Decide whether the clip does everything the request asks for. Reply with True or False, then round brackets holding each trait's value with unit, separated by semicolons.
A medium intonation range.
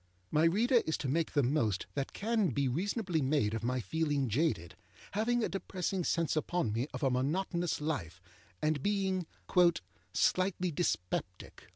False (6.3 semitones)